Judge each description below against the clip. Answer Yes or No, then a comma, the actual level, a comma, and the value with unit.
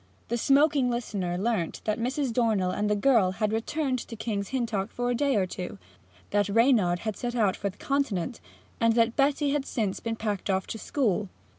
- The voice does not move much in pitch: No, average, 3.9 semitones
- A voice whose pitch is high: Yes, high, 225 Hz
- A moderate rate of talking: Yes, average, 195 wpm